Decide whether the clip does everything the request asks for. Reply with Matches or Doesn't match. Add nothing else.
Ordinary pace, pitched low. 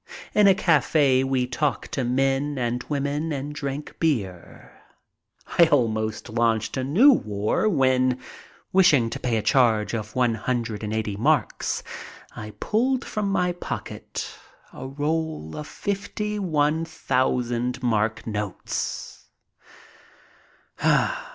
Doesn't match